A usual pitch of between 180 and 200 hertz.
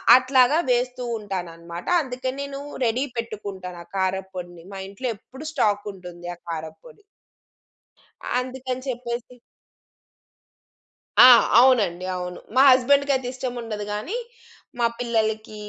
No: high, 230 Hz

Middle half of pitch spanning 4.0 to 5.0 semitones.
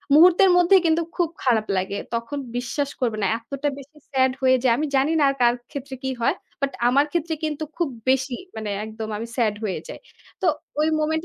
Yes: average, 4.5 semitones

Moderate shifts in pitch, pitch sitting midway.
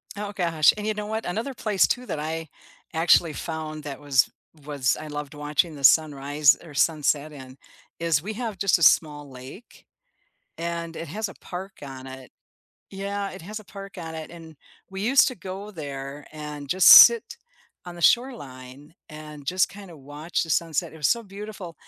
Yes: average, 5.0 semitones; medium, 165 Hz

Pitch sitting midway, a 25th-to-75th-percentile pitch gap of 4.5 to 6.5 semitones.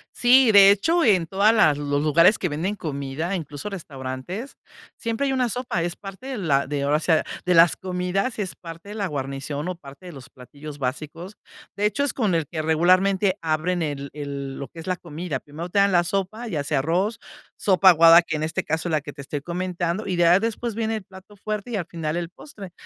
Yes: medium, 175 Hz; average, 4.8 semitones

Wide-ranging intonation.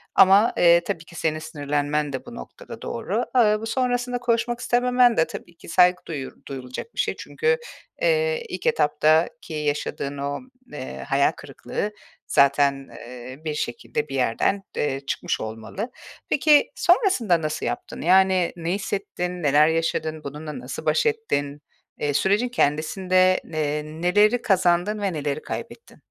Yes: wide, 7.7 semitones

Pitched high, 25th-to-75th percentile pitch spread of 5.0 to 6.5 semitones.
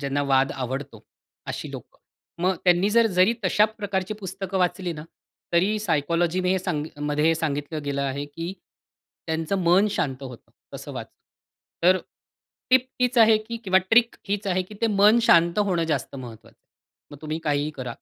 No: medium, 175 Hz; average, 5.3 semitones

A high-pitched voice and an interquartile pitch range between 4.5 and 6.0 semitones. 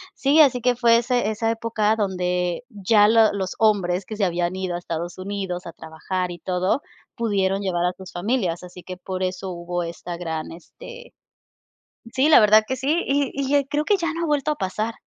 Yes: high, 200 Hz; average, 5.1 semitones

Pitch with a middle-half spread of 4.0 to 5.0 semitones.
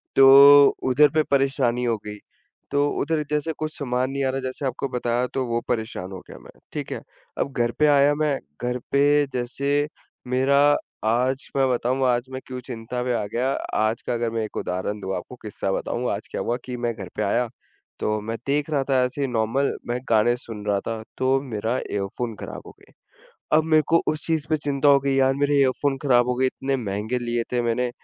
No: average, 3.0 semitones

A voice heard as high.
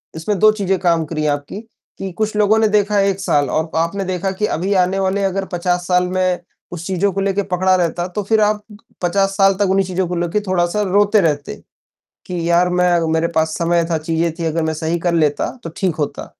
No: medium, 180 Hz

